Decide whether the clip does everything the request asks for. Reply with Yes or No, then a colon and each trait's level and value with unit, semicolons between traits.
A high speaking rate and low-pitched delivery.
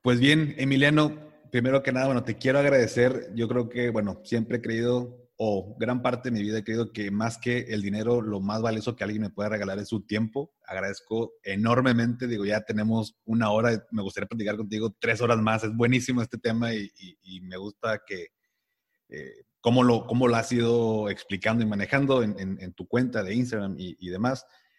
Yes: fast, 210 wpm; low, 115 Hz